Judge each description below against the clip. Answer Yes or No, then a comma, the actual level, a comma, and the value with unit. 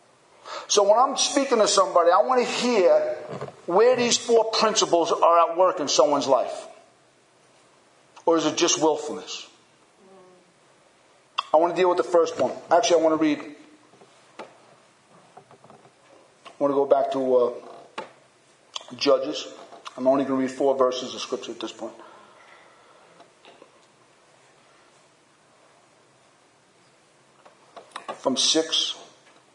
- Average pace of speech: No, slow, 120 wpm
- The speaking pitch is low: No, medium, 170 Hz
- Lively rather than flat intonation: Yes, wide, 5.7 semitones